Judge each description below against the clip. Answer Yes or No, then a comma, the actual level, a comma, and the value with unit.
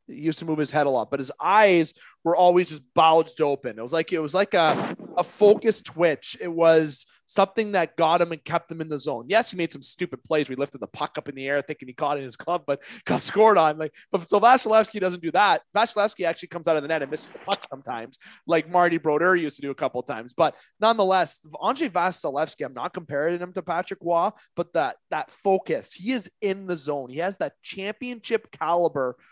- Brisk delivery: Yes, fast, 240 wpm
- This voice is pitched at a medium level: Yes, medium, 165 Hz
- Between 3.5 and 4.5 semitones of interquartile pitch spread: Yes, average, 4.0 semitones